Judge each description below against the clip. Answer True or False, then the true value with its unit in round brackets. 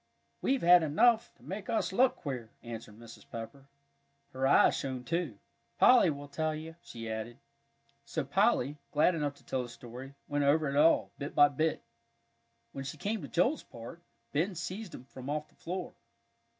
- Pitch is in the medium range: True (145 Hz)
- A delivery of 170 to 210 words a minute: True (175 wpm)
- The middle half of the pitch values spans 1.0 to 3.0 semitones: False (5.1 semitones)